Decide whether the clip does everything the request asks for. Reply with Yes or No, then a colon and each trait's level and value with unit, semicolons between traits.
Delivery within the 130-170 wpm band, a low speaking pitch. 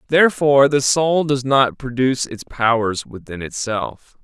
Yes: average, 140 wpm; low, 130 Hz